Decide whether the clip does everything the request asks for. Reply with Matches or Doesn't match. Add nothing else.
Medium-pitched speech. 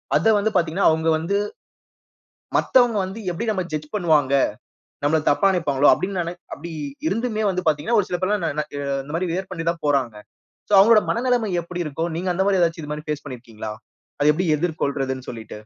Matches